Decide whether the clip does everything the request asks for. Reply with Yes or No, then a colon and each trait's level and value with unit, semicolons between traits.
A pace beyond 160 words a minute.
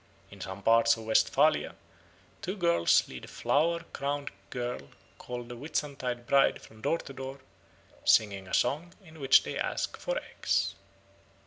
No: average, 150 wpm